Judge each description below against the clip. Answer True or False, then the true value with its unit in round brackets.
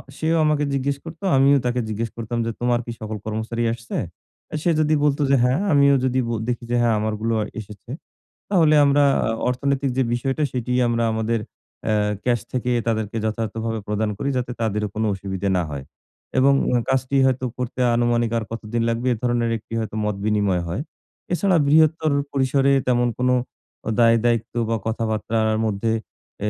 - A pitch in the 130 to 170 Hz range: False (120 Hz)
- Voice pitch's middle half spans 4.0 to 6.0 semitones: False (3.3 semitones)